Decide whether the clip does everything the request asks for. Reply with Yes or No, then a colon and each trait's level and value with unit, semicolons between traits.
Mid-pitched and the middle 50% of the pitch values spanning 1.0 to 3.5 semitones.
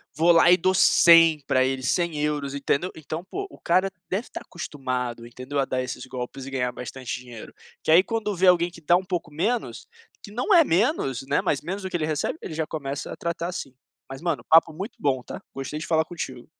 No: medium, 155 Hz; average, 4.9 semitones